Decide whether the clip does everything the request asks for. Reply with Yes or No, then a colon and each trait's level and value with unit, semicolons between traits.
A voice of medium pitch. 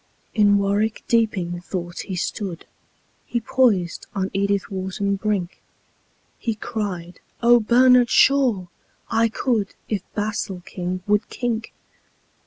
No: high, 205 Hz